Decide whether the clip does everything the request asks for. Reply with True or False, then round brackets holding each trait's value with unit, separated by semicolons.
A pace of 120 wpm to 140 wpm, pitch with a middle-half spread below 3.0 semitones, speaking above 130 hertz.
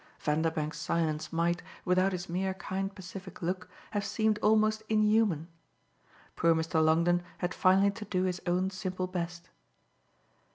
True (135 wpm; 2.6 semitones; 185 Hz)